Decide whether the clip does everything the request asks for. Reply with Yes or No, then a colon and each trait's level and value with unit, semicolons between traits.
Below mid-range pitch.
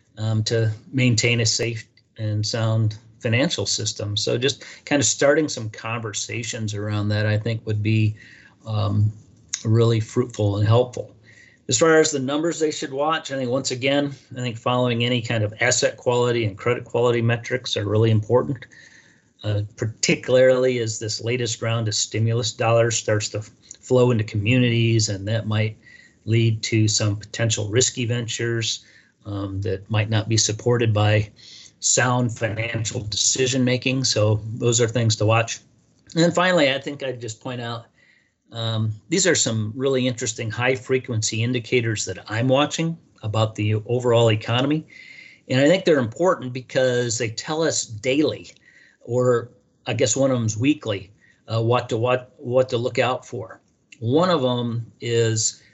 Yes: low, 115 Hz